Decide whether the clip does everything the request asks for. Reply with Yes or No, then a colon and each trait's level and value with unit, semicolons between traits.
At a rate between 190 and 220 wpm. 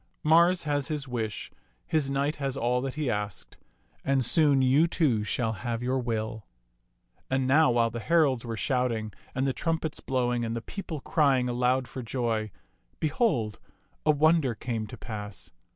No: average, 165 wpm